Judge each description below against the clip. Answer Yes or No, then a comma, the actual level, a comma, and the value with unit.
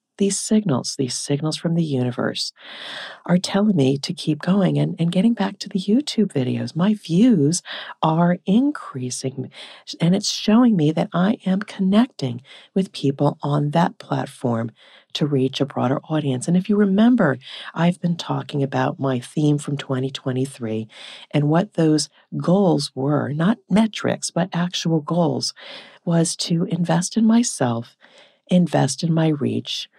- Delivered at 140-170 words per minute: Yes, average, 150 wpm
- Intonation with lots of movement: Yes, wide, 6.0 semitones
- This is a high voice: No, medium, 165 Hz